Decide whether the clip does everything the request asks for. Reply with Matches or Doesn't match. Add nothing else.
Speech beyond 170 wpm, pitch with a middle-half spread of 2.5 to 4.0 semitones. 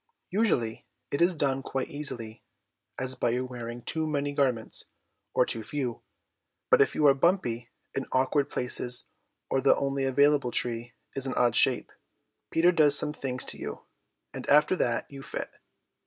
Doesn't match